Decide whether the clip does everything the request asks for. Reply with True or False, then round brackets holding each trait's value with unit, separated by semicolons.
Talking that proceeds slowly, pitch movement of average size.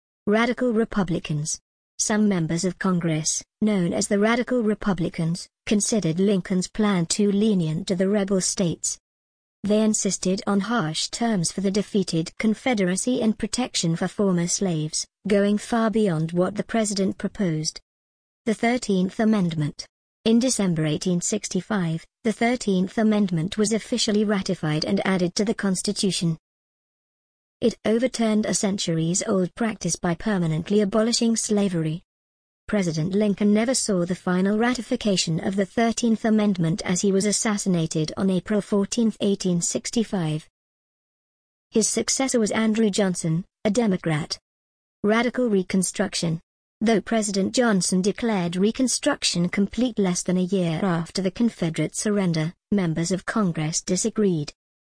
True (125 wpm; 3.6 semitones)